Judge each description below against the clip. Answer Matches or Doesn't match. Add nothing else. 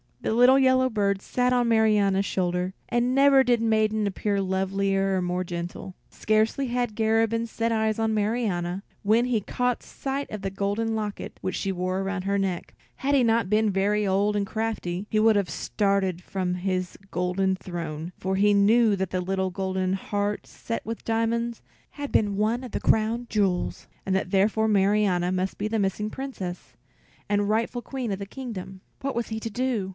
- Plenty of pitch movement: Doesn't match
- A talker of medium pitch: Doesn't match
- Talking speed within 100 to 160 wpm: Doesn't match